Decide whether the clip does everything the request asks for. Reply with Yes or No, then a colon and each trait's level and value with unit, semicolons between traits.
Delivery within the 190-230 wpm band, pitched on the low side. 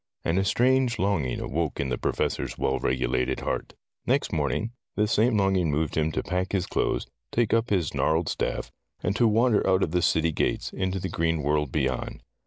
Yes: average, 195 wpm; very low, 90 Hz